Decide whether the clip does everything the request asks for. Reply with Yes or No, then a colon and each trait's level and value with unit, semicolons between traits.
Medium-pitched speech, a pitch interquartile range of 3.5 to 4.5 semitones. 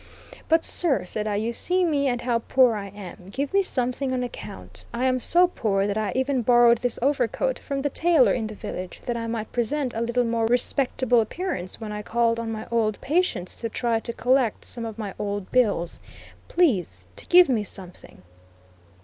No: high, 235 Hz; average, 3.8 semitones